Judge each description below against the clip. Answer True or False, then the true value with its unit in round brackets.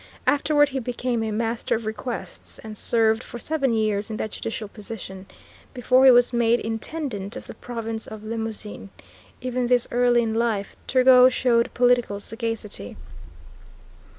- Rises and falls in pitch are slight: True (2.2 semitones)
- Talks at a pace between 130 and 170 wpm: True (150 wpm)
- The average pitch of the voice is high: True (230 Hz)